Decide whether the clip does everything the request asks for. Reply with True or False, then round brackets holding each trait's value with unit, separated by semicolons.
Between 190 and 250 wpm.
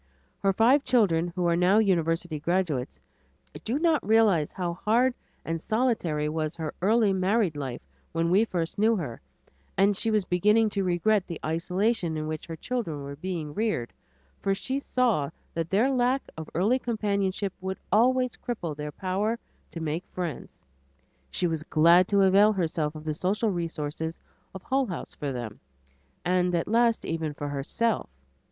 False (165 wpm)